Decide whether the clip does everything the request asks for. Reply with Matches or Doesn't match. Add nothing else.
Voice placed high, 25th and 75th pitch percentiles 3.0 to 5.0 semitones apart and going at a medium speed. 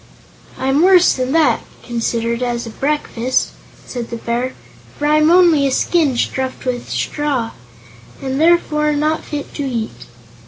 Matches